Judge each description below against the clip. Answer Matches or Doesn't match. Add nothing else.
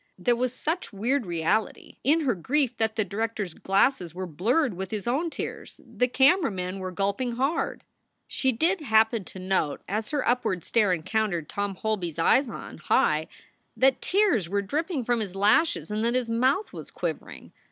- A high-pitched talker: Matches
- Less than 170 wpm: Doesn't match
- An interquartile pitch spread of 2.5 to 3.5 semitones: Doesn't match